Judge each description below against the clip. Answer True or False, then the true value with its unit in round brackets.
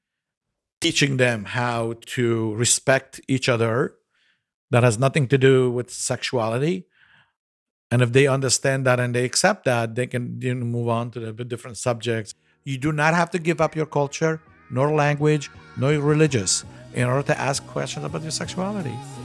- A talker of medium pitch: False (125 Hz)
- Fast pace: False (170 wpm)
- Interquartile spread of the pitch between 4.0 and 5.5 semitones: False (3.3 semitones)